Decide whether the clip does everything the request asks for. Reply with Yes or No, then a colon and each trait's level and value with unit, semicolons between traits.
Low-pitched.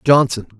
Yes: low, 120 Hz